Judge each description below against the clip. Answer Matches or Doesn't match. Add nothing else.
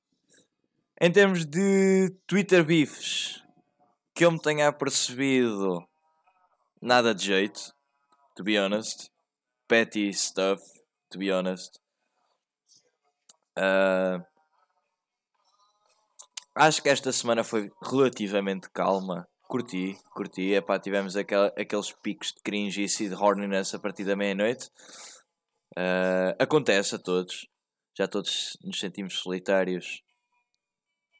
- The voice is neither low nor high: Doesn't match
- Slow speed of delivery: Matches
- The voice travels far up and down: Matches